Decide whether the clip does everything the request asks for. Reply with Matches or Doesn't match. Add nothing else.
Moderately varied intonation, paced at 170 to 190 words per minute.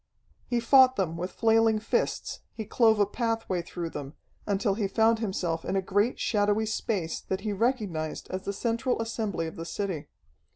Matches